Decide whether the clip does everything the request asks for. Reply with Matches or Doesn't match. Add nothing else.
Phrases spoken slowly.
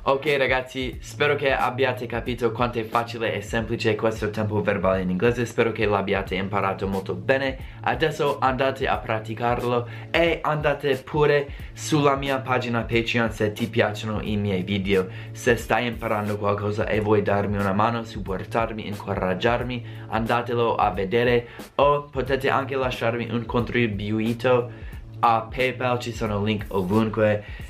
Doesn't match